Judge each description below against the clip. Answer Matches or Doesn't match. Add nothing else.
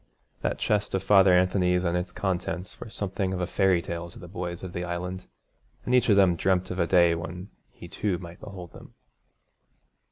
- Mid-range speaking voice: Doesn't match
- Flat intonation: Matches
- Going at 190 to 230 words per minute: Matches